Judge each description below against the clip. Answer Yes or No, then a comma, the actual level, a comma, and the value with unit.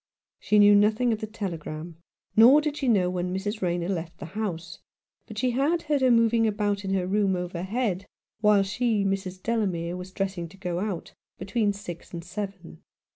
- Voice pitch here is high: Yes, high, 195 Hz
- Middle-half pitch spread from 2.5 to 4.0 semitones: Yes, average, 3.4 semitones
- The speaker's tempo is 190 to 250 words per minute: Yes, average, 195 wpm